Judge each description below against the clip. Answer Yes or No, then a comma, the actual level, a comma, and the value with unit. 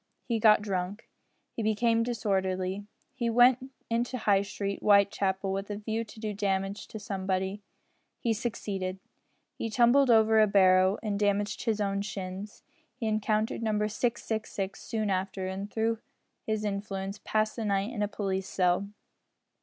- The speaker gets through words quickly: No, average, 150 wpm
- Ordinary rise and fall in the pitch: No, narrow, 2.2 semitones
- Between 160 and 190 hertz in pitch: No, high, 205 Hz